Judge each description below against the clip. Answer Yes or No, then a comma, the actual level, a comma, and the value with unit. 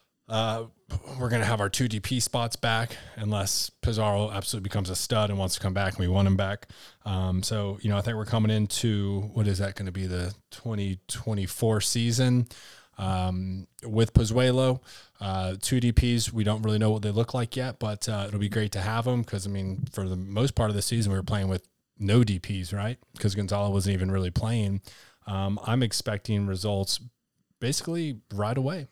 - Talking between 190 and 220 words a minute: Yes, average, 200 wpm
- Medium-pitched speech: No, low, 105 Hz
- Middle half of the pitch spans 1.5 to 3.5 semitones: Yes, average, 2.9 semitones